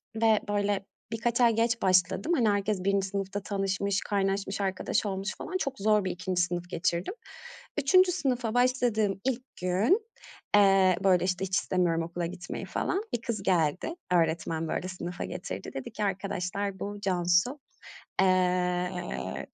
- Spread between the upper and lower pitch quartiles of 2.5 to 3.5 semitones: Yes, average, 3.2 semitones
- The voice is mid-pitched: No, high, 195 Hz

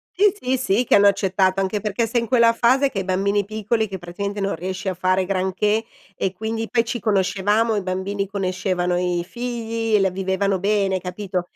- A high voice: Yes, high, 200 Hz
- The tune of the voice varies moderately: Yes, average, 3.0 semitones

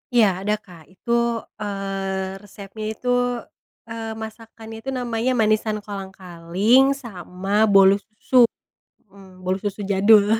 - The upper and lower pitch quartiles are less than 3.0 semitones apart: Yes, narrow, 2.6 semitones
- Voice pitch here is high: Yes, high, 205 Hz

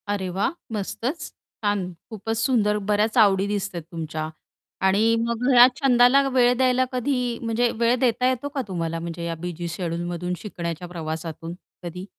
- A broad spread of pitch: Yes, wide, 5.9 semitones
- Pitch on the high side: Yes, high, 205 Hz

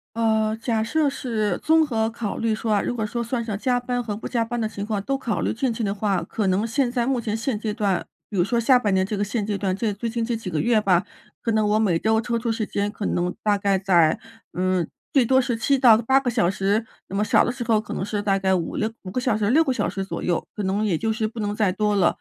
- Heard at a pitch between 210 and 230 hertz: Yes, high, 220 Hz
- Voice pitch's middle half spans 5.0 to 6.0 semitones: No, average, 2.8 semitones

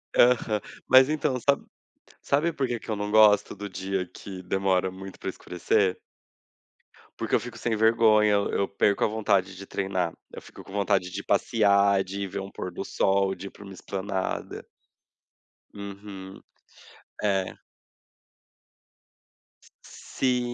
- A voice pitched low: Yes, low, 100 Hz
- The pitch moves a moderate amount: No, narrow, 2.2 semitones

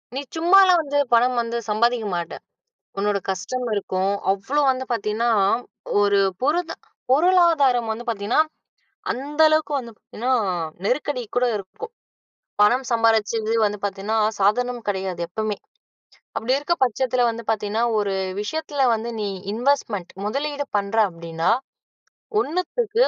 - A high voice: Yes, high, 235 Hz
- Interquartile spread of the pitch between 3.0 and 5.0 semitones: No, wide, 5.4 semitones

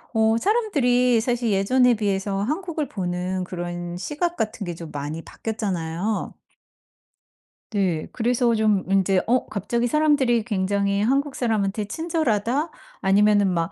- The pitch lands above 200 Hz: Yes, high, 215 Hz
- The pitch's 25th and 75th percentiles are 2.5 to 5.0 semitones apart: Yes, average, 4.5 semitones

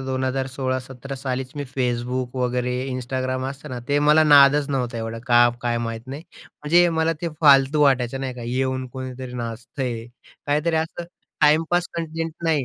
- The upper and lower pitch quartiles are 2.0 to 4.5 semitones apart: Yes, average, 2.9 semitones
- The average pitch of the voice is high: No, low, 130 Hz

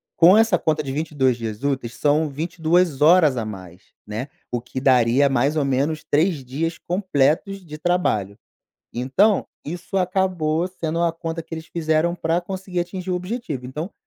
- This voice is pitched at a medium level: Yes, medium, 155 Hz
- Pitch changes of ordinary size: Yes, average, 4.8 semitones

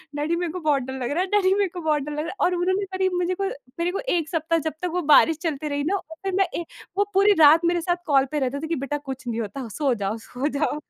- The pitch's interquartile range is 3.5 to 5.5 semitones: Yes, average, 4.0 semitones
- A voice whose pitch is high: Yes, very high, 320 Hz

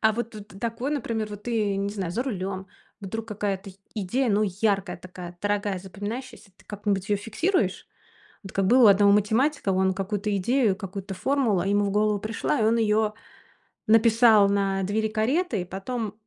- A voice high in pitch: Yes, high, 205 Hz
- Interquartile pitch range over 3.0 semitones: No, narrow, 2.5 semitones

